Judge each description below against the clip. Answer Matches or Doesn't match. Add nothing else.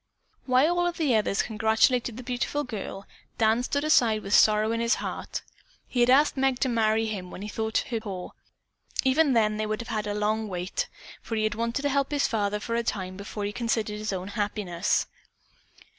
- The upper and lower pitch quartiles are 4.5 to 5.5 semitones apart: Doesn't match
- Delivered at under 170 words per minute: Doesn't match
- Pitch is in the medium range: Doesn't match